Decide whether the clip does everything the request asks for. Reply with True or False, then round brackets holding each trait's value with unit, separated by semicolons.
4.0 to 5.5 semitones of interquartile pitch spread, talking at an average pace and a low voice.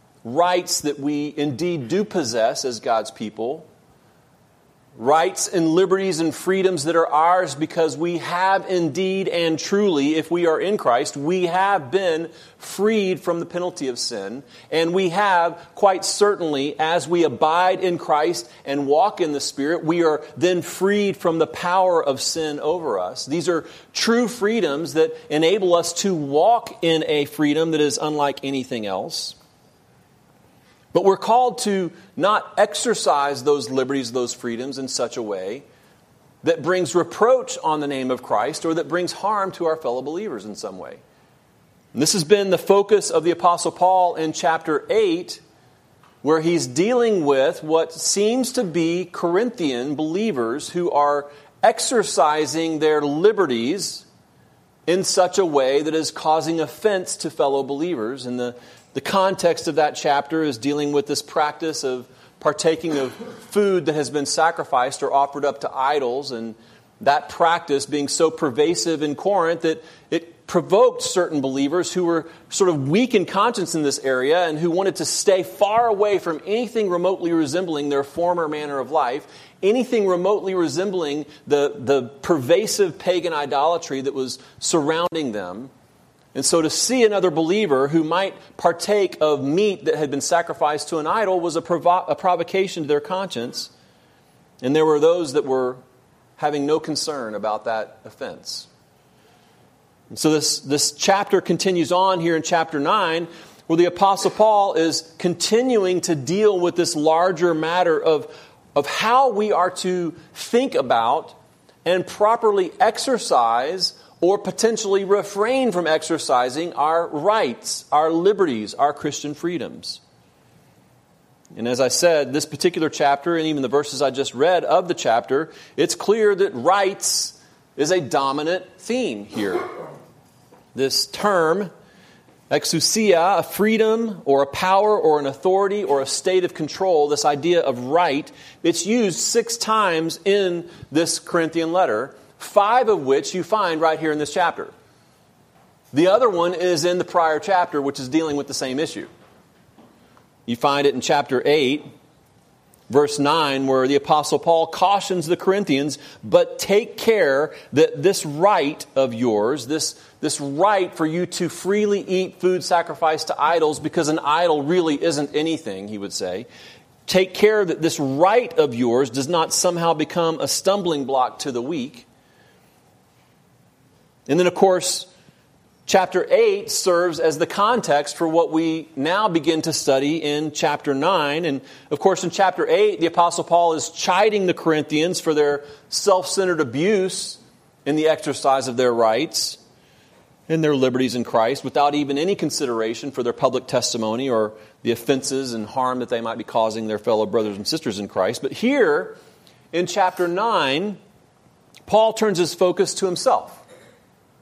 False (4.4 semitones; 160 wpm; 165 Hz)